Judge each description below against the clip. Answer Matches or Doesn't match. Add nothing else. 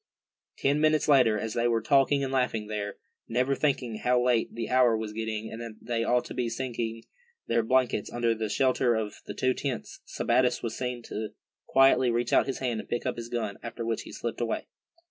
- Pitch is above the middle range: Doesn't match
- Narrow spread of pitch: Matches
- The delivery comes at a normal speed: Doesn't match